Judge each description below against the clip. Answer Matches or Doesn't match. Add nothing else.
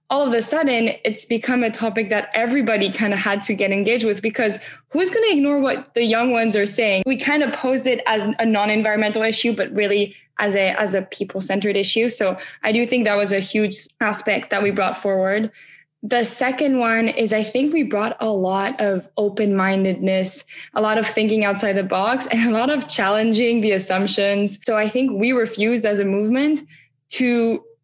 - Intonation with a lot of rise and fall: Doesn't match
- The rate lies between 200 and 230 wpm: Matches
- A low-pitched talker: Doesn't match